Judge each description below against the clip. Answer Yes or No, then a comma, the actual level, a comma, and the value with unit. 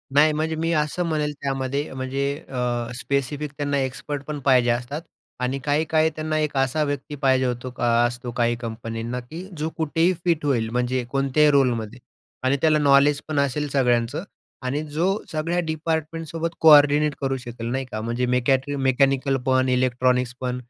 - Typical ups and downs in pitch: Yes, average, 3.3 semitones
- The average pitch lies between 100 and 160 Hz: Yes, medium, 140 Hz